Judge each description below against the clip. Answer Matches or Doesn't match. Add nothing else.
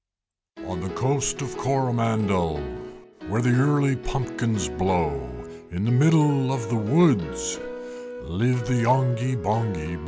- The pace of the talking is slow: Matches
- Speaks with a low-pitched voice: Matches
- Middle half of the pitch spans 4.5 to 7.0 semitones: Matches